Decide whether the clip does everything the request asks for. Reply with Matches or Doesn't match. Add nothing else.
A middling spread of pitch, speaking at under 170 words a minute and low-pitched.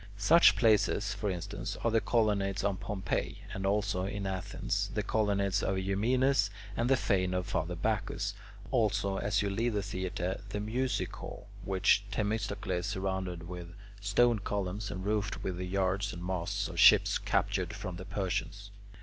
Doesn't match